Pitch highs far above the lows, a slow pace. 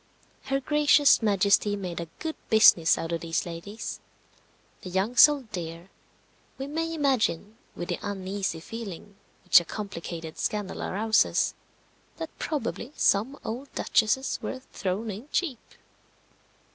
Yes: wide, 6.5 semitones; slow, 130 wpm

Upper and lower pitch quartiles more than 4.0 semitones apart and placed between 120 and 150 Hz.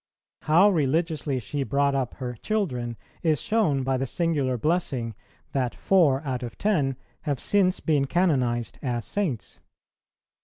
Yes: average, 4.9 semitones; medium, 140 Hz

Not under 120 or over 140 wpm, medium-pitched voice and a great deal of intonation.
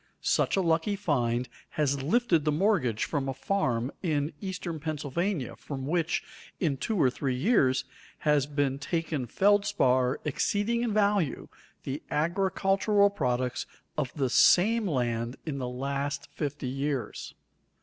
Yes: slow, 135 wpm; medium, 150 Hz; wide, 6.2 semitones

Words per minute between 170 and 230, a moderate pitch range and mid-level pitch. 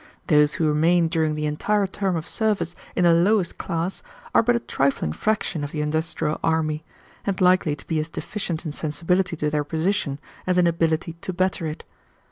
Yes: average, 190 wpm; average, 3.1 semitones; medium, 165 Hz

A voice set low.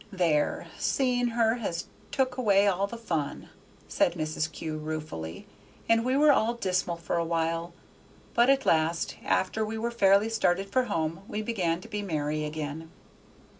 No: high, 190 Hz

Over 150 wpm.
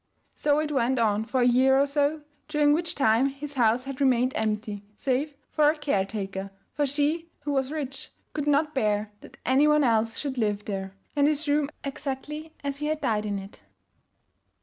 Yes: average, 190 wpm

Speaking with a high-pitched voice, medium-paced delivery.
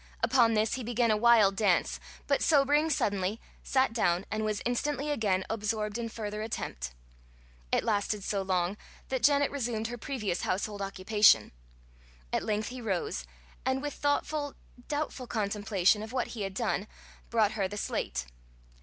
Yes: high, 220 Hz; average, 155 wpm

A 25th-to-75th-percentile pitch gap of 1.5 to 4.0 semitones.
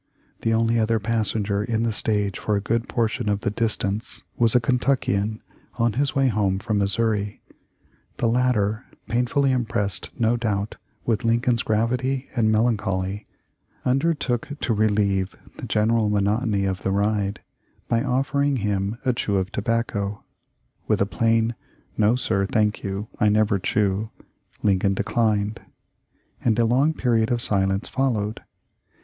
Yes: narrow, 2.5 semitones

